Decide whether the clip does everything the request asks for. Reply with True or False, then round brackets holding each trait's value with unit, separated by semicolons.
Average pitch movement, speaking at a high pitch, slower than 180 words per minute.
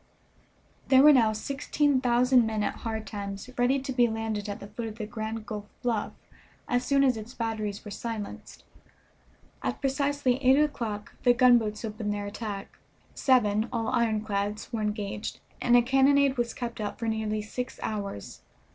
True (3.0 semitones; 225 Hz; 165 wpm)